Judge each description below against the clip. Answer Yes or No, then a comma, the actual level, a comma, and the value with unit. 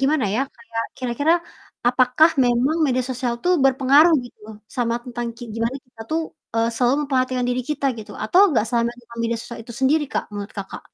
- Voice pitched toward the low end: No, very high, 250 Hz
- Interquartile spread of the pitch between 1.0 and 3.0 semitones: Yes, narrow, 2.4 semitones